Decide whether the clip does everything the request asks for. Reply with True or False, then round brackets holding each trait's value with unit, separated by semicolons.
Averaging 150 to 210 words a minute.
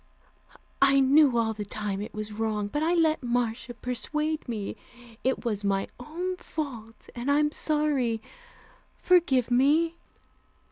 False (135 wpm)